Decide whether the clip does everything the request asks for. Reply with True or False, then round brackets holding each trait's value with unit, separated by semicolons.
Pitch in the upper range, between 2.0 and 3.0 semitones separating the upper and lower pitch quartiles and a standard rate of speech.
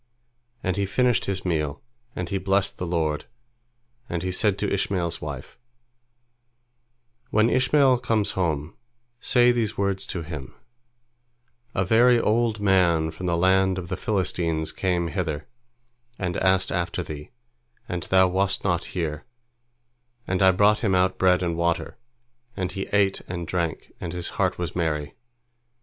False (90 Hz; 2.6 semitones; 150 wpm)